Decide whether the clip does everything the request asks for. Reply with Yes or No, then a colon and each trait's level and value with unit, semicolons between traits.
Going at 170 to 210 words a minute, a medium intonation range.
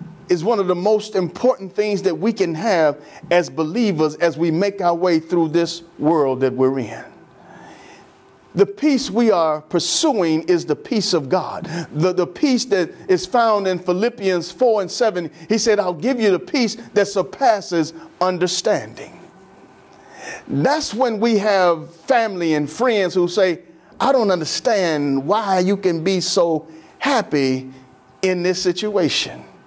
No: average, 155 wpm; average, 3.9 semitones